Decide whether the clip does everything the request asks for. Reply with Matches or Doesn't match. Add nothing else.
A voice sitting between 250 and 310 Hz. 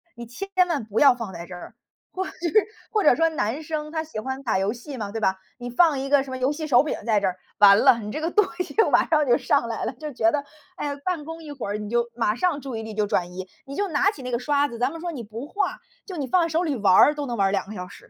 Matches